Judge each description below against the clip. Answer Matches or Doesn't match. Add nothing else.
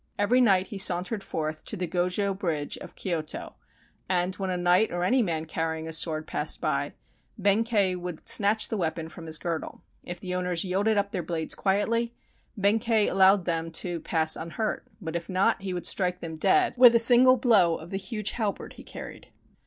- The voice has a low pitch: Doesn't match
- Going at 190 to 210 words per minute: Matches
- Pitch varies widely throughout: Doesn't match